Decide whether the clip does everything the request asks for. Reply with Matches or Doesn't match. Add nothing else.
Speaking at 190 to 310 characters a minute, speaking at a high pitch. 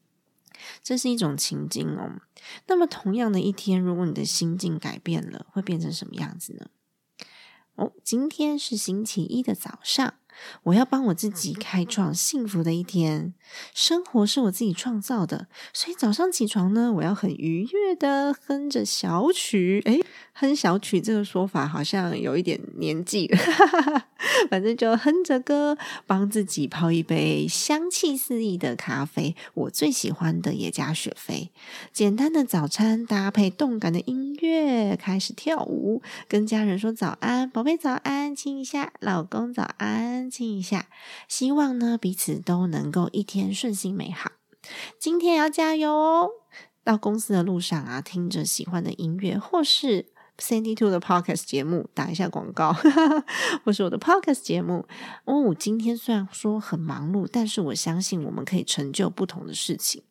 Matches